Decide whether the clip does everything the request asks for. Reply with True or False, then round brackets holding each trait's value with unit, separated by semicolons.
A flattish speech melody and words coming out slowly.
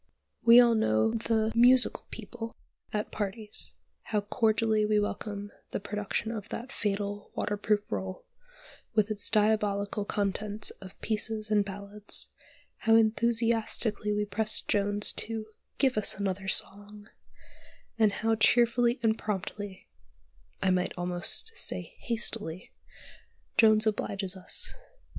True (1.8 semitones; 120 wpm)